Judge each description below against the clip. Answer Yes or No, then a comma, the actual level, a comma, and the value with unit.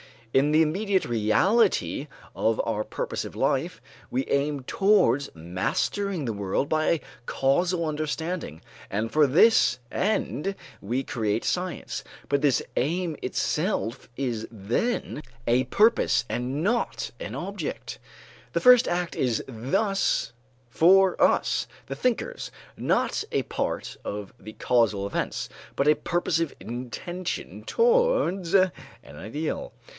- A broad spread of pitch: Yes, wide, 7.9 semitones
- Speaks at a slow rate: Yes, slow, 120 wpm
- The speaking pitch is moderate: Yes, medium, 150 Hz